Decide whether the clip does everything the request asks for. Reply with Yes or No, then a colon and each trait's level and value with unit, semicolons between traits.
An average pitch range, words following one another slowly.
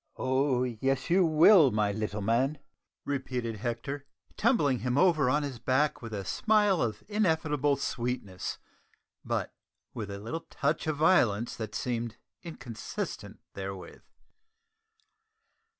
Yes: average, 4.9 semitones; slow, 120 wpm